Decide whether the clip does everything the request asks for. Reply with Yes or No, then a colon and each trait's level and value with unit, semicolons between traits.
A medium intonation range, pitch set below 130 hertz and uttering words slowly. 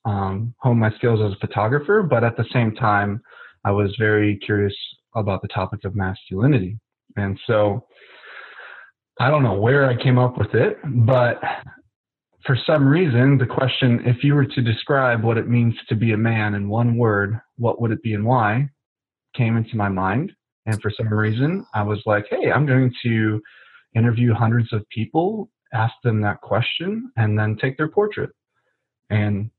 No: average, 3.4 semitones; low, 115 Hz; average, 180 wpm